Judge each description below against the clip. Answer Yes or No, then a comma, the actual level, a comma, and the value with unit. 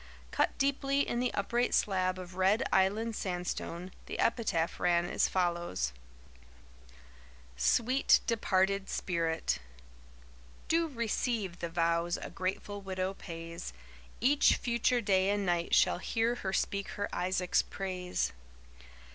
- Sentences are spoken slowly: Yes, slow, 120 wpm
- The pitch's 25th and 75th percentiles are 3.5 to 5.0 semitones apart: Yes, average, 4.5 semitones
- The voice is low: No, high, 190 Hz